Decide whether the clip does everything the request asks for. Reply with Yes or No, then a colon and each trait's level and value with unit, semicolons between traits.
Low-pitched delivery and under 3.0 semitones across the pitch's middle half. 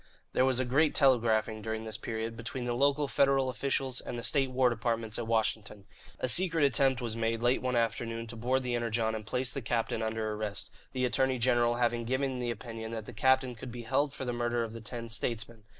Yes: low, 120 Hz; narrow, 2.4 semitones